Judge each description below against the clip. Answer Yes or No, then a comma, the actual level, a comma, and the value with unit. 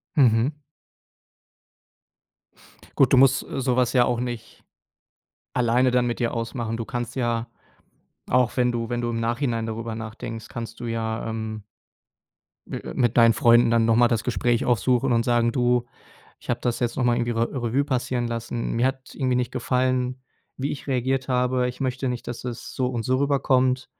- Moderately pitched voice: No, low, 120 Hz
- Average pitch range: No, narrow, 1.7 semitones